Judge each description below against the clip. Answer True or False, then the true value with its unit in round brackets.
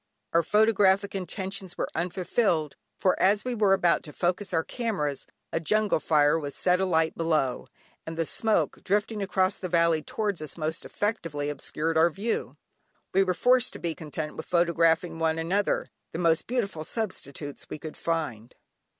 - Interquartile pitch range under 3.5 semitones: False (3.8 semitones)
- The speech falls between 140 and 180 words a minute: True (165 wpm)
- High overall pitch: False (170 Hz)